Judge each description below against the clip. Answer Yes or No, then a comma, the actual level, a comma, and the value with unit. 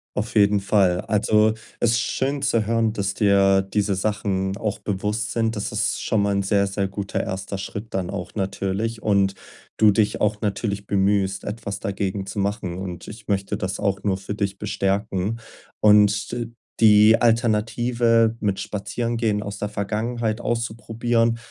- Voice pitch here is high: No, low, 105 Hz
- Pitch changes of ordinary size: No, narrow, 2.2 semitones